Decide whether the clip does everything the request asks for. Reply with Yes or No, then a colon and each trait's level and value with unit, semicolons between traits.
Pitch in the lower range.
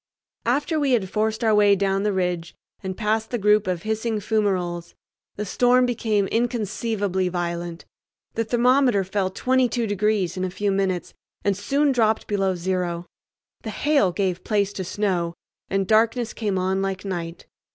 No: high, 205 Hz